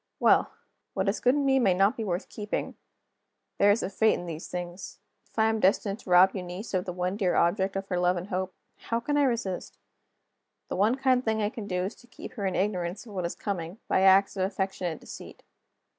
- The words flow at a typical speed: No, fast, 230 wpm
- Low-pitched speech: No, high, 195 Hz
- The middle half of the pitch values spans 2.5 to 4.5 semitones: Yes, average, 3.3 semitones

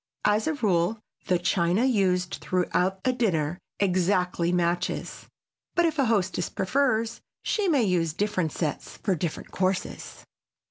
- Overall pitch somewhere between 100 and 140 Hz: No, medium, 185 Hz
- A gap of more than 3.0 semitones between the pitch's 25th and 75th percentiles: Yes, average, 4.0 semitones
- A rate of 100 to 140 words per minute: Yes, slow, 135 wpm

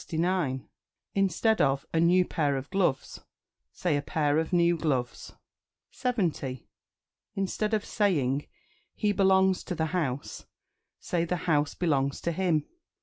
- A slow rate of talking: Yes, slow, 130 wpm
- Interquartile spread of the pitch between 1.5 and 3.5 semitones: No, average, 4.7 semitones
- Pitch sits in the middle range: Yes, medium, 170 Hz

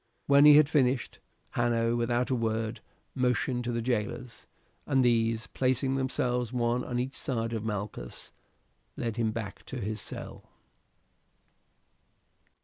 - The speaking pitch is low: Yes, low, 120 Hz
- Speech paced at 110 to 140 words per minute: Yes, slow, 135 wpm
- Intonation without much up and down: Yes, narrow, 2.1 semitones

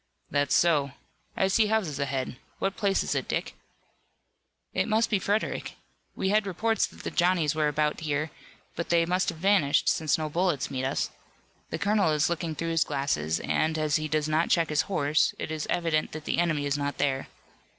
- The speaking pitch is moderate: Yes, medium, 155 Hz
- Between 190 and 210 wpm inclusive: Yes, average, 195 wpm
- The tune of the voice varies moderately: Yes, average, 3.9 semitones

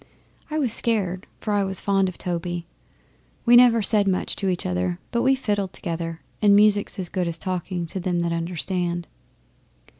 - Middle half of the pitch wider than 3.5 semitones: No, average, 3.1 semitones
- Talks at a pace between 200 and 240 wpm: No, average, 180 wpm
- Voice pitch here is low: No, medium, 185 Hz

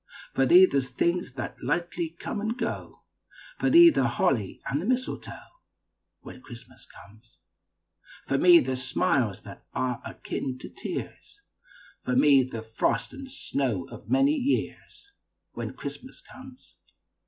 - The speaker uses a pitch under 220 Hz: Yes, medium, 140 Hz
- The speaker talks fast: No, average, 140 wpm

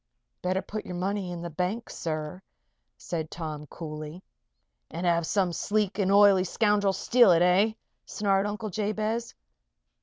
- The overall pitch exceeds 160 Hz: Yes, high, 190 Hz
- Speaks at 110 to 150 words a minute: Yes, average, 145 wpm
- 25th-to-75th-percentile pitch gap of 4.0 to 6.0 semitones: No, average, 3.4 semitones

